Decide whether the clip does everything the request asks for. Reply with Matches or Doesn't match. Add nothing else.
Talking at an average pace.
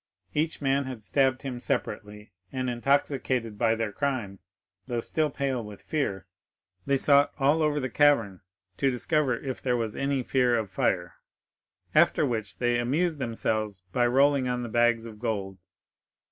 Matches